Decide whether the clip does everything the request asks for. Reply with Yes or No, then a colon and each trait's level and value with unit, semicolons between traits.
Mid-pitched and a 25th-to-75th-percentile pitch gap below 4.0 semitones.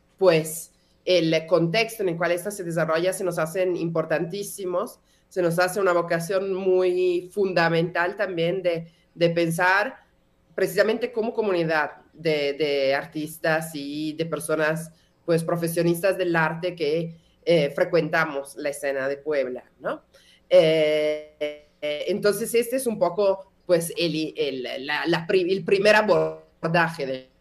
Yes: medium, 170 Hz; average, 2.9 semitones